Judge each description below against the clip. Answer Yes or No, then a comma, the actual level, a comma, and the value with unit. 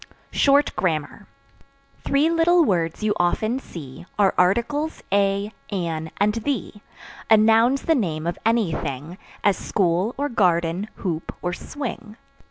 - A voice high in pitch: Yes, high, 205 Hz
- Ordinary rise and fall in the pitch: No, wide, 5.7 semitones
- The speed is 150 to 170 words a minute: No, slow, 135 wpm